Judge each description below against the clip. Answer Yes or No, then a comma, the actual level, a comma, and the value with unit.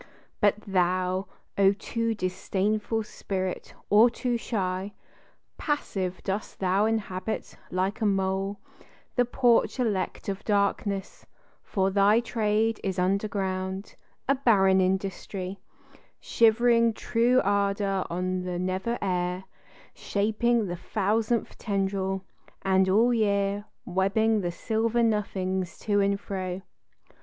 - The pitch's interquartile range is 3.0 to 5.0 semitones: No, narrow, 2.6 semitones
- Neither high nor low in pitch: No, high, 200 Hz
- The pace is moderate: No, slow, 110 wpm